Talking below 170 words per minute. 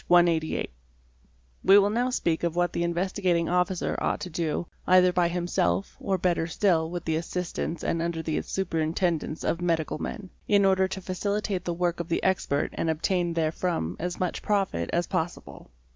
No: average, 175 wpm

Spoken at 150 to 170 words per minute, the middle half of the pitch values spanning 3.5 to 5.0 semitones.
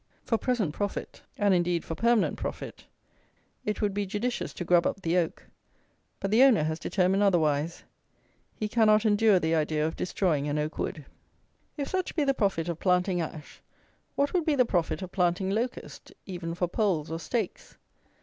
No: average, 180 wpm; average, 4.5 semitones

